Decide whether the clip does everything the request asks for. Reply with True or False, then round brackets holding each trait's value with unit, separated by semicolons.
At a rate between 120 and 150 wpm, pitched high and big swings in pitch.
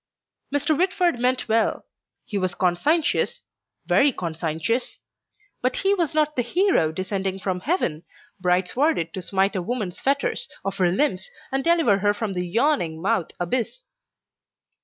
True (145 wpm; 220 Hz; 8.1 semitones)